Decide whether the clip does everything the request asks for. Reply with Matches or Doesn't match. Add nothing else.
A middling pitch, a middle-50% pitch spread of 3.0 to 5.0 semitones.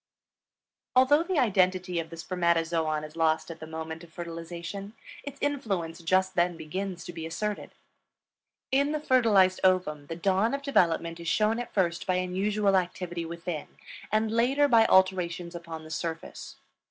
Matches